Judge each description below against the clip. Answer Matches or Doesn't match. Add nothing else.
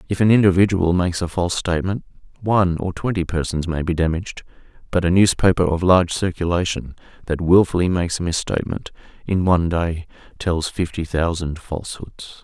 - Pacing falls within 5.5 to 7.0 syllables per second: Matches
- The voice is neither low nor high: Doesn't match